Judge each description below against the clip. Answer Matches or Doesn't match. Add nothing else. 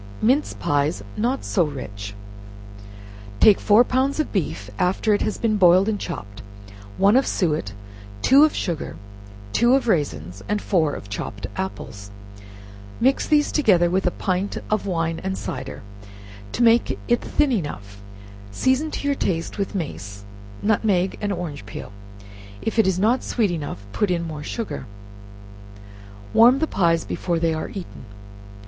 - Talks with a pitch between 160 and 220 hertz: Matches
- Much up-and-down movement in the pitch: Matches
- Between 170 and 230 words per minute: Doesn't match